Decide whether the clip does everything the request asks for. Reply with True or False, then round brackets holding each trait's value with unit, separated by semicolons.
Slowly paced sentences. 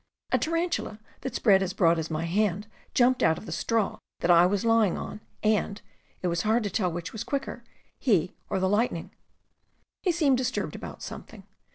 False (195 wpm)